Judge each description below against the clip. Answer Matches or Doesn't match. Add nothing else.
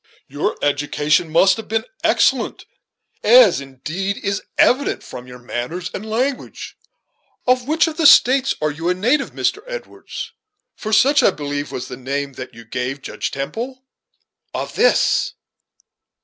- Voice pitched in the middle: Matches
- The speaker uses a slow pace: Doesn't match